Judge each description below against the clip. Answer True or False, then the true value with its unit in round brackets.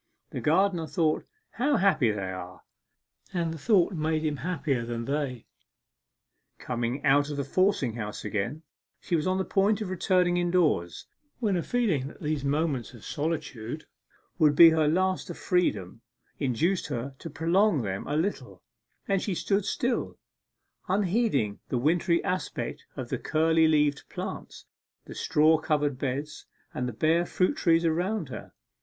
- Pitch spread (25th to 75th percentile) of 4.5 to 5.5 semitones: True (4.9 semitones)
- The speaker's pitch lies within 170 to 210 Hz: False (155 Hz)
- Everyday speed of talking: True (155 wpm)